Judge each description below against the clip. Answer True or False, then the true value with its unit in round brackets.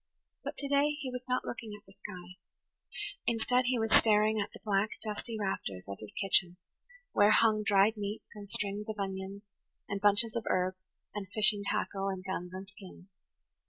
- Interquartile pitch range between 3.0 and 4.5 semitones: False (2.4 semitones)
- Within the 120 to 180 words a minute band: True (175 wpm)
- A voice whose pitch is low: False (205 Hz)